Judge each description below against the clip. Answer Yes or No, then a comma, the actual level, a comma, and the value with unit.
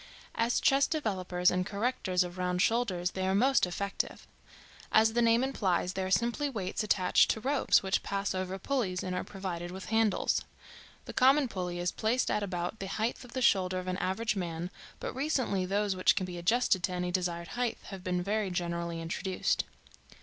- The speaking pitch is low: No, high, 190 Hz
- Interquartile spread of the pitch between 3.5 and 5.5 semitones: Yes, average, 4.0 semitones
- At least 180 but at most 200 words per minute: Yes, average, 190 wpm